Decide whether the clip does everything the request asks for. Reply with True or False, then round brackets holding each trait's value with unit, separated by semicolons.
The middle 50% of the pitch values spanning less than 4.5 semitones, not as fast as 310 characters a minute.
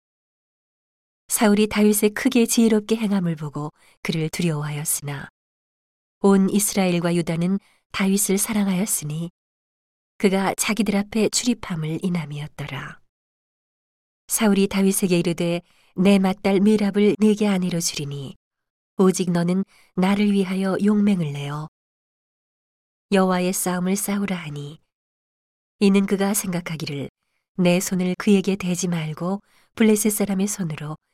True (2.9 semitones; 270 characters per minute)